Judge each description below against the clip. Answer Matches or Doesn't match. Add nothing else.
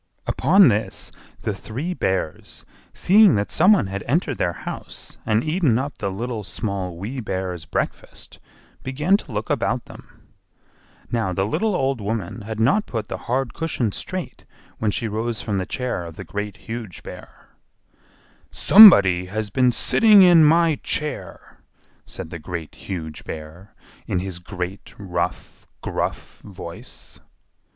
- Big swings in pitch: Matches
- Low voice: Matches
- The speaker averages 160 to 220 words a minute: Doesn't match